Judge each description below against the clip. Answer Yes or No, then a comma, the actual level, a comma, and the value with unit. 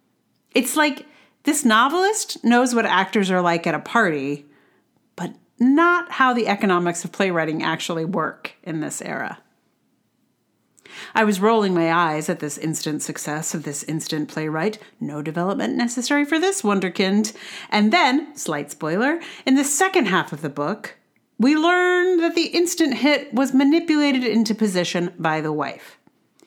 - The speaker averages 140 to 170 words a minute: Yes, average, 150 wpm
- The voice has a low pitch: No, high, 215 Hz